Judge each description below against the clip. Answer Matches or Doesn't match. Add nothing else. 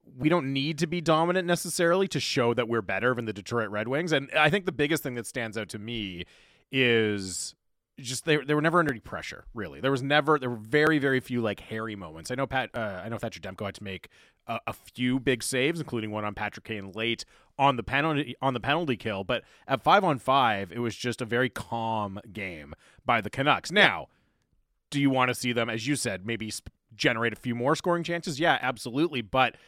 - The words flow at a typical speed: Doesn't match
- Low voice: Matches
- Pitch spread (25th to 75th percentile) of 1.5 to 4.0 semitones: Doesn't match